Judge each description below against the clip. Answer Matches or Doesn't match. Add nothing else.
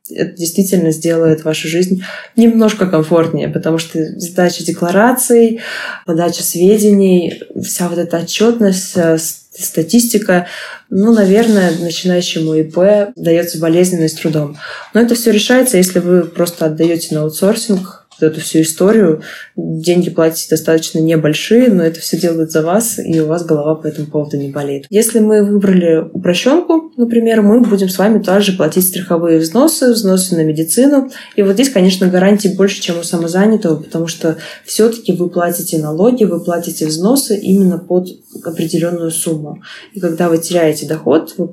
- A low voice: Doesn't match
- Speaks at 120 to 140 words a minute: Doesn't match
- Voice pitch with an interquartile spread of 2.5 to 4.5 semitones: Matches